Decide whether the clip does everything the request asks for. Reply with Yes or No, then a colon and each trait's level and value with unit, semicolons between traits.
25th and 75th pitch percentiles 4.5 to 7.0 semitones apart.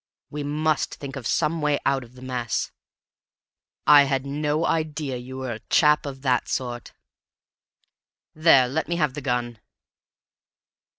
No: average, 2.9 semitones